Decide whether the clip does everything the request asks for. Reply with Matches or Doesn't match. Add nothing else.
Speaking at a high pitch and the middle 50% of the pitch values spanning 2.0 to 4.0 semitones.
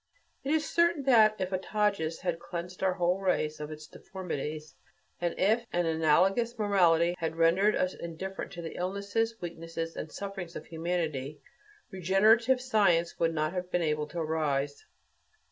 Doesn't match